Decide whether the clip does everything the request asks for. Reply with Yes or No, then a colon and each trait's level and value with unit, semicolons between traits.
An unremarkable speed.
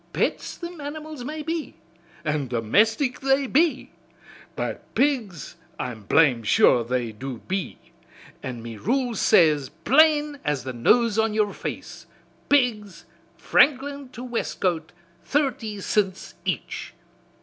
No: slow, 120 wpm